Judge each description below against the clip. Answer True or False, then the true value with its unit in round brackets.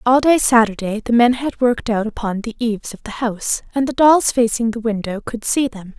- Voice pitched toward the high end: True (235 Hz)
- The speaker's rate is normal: False (230 wpm)